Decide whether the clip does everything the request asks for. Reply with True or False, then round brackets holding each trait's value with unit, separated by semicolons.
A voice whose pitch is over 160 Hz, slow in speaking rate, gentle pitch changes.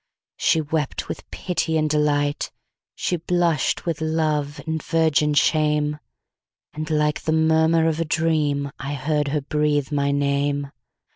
False (150 Hz; 125 wpm; 1.6 semitones)